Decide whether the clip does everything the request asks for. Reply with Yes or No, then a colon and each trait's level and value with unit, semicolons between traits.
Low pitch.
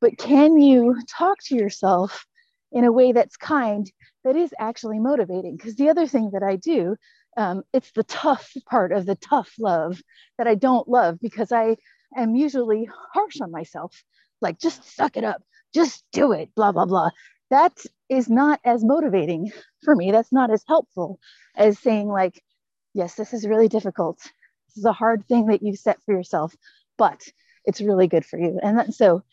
No: high, 230 Hz